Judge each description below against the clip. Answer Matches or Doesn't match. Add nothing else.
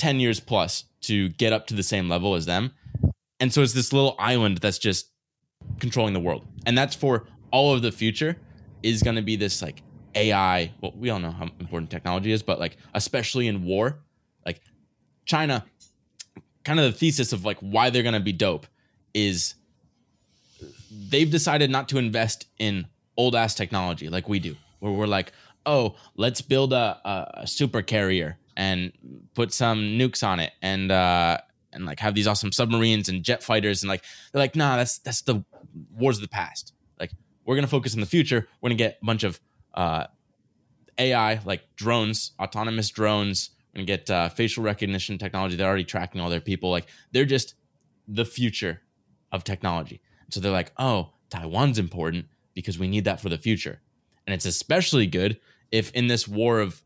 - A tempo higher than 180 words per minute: Matches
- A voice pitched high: Doesn't match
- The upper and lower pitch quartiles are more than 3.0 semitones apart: Matches